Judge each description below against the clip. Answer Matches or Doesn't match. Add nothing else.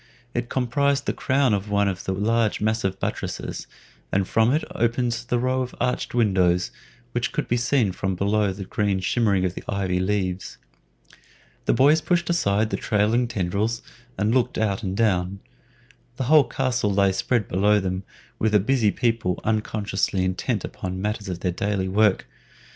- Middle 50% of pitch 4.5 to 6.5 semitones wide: Doesn't match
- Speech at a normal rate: Matches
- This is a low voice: Matches